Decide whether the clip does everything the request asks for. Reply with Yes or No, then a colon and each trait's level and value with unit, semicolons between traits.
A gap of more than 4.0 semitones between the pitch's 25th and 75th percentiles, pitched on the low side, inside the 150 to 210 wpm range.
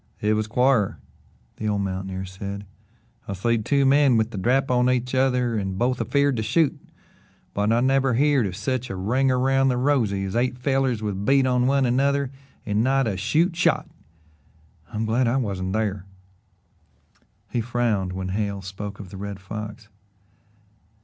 Yes: average, 4.5 semitones; low, 115 Hz; average, 170 wpm